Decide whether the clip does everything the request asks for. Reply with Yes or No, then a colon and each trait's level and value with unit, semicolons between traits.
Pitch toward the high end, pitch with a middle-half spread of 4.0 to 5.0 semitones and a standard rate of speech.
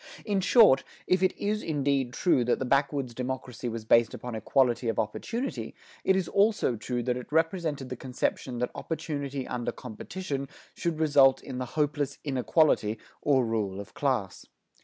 No: low, 135 Hz; average, 4.4 semitones; average, 160 wpm